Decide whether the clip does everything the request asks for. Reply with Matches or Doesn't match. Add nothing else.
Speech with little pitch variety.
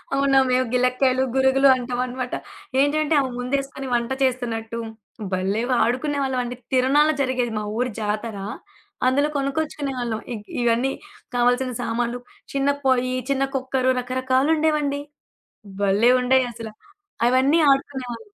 Matches